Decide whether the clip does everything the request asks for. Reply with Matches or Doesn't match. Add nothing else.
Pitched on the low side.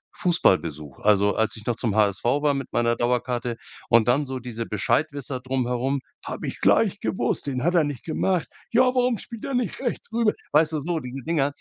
Matches